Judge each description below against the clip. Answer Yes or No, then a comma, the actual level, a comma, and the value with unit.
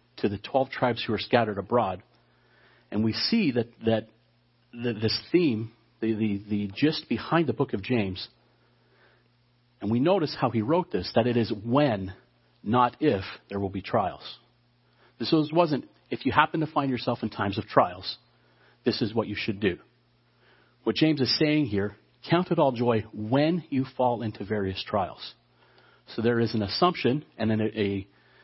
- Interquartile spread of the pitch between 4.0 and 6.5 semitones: No, average, 3.5 semitones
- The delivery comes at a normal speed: Yes, average, 180 wpm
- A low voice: Yes, low, 120 Hz